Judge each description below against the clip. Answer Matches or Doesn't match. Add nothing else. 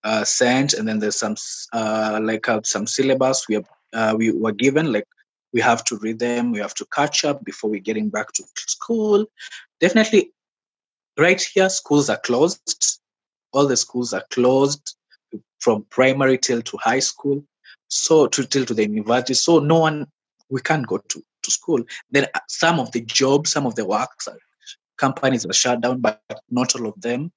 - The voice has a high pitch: Doesn't match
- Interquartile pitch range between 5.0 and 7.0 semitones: Doesn't match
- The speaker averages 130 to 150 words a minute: Doesn't match